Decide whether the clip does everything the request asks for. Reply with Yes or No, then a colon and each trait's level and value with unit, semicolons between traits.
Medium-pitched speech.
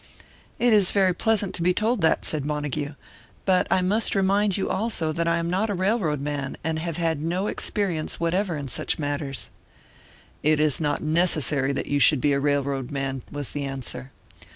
Yes: medium, 160 Hz